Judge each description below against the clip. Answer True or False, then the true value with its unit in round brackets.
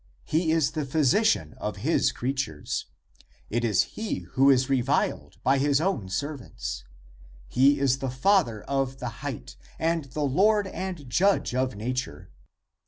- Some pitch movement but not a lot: True (4.3 semitones)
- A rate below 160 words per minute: True (150 wpm)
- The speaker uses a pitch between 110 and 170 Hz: True (135 Hz)